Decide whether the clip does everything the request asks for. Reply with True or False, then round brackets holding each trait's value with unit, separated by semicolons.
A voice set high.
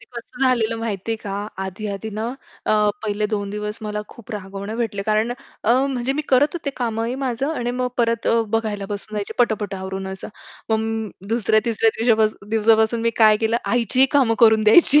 True (220 Hz)